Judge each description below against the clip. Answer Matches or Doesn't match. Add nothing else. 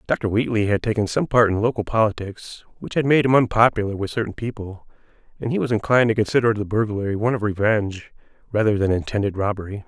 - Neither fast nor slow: Matches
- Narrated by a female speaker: Doesn't match